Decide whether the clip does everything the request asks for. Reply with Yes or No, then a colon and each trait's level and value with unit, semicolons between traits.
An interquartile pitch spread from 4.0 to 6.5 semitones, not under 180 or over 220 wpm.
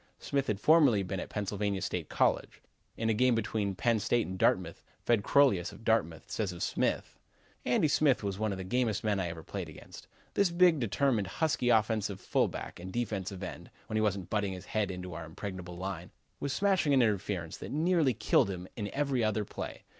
Yes: average, 4.6 semitones; average, 200 wpm